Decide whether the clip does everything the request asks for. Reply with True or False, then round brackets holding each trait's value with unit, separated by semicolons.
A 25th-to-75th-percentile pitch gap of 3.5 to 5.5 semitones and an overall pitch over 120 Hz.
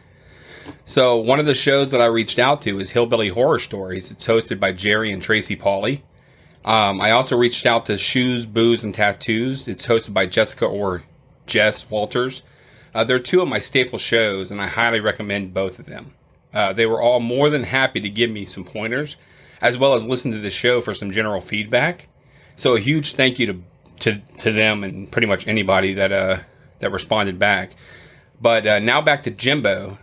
False (3.8 semitones; 115 Hz)